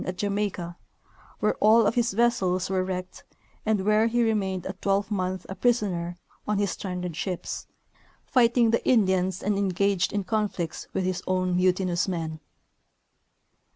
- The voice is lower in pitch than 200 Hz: Yes, high, 190 Hz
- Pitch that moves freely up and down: No, narrow, 2.6 semitones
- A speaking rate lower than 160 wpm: Yes, average, 145 wpm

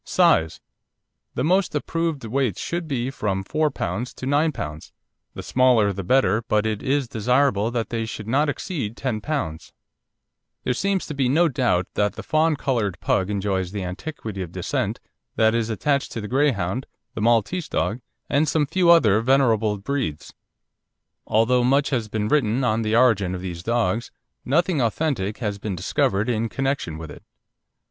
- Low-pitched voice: Yes, low, 115 Hz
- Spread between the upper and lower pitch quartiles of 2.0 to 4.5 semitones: No, average, 5.2 semitones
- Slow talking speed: No, average, 170 wpm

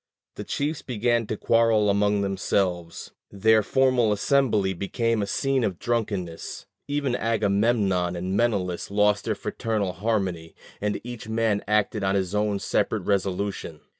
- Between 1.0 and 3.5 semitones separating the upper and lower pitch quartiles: Yes, average, 2.9 semitones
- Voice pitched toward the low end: Yes, low, 105 Hz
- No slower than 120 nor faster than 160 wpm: Yes, slow, 135 wpm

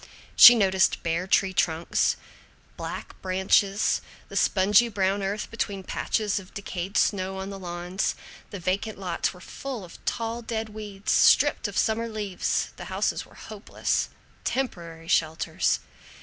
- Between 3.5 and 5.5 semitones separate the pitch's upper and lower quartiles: No, average, 2.8 semitones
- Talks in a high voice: Yes, high, 195 Hz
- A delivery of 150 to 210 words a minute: No, average, 140 wpm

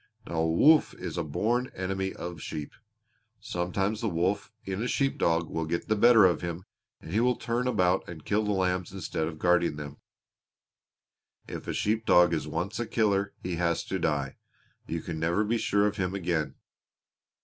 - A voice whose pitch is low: Yes, very low, 90 Hz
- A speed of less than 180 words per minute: No, average, 190 wpm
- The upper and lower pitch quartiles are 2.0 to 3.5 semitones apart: No, average, 4.0 semitones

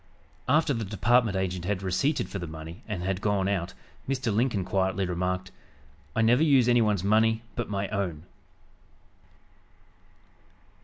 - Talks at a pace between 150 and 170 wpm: No, average, 140 wpm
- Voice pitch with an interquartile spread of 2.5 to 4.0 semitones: Yes, average, 3.7 semitones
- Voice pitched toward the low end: Yes, low, 100 Hz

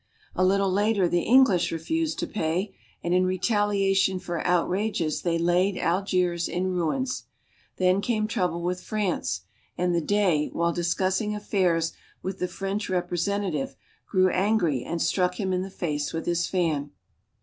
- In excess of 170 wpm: No, average, 155 wpm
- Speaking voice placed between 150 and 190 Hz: Yes, medium, 185 Hz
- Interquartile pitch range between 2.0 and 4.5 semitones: Yes, narrow, 2.6 semitones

